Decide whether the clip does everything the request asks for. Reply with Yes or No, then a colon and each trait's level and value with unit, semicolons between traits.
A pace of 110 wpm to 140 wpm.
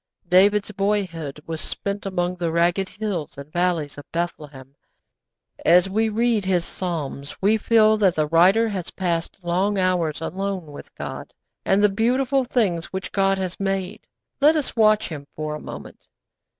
No: average, 160 wpm